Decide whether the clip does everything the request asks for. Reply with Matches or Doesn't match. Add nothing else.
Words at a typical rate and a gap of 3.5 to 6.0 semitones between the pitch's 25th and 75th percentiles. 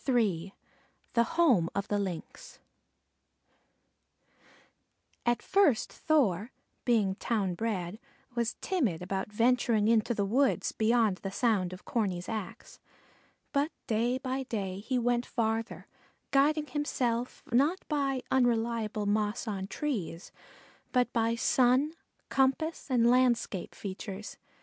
Doesn't match